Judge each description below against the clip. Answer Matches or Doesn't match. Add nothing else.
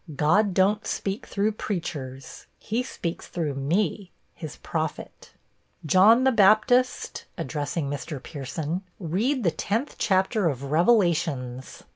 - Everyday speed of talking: Doesn't match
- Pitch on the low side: Doesn't match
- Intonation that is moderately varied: Doesn't match